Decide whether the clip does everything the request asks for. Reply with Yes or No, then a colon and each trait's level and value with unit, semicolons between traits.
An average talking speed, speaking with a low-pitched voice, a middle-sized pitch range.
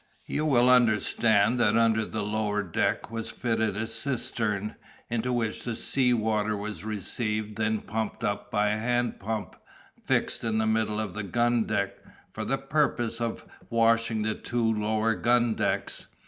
No: average, 165 wpm; low, 110 Hz; narrow, 1.6 semitones